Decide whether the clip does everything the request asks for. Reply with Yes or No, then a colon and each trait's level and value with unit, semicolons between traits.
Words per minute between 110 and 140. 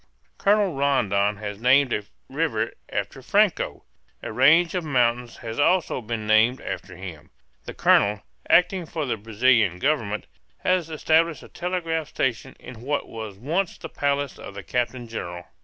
No: average, 155 wpm